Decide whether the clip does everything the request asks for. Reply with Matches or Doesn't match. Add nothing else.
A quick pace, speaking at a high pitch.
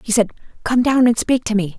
Matches